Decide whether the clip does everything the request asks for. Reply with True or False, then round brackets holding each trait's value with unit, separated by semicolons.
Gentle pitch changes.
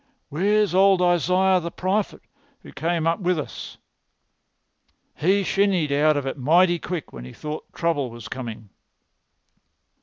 False (4.4 semitones)